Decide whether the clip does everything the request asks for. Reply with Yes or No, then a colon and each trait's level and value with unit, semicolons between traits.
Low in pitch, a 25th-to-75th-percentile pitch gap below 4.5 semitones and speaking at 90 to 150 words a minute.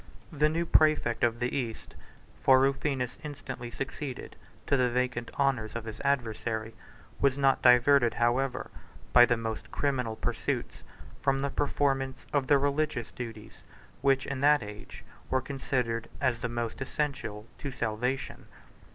Yes: low, 130 Hz; average, 2.9 semitones; average, 145 wpm